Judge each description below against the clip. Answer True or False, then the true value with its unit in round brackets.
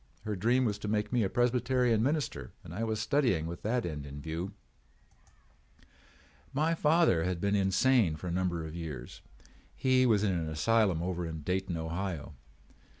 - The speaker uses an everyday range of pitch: False (6.3 semitones)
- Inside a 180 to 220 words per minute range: False (170 wpm)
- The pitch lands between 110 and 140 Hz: False (100 Hz)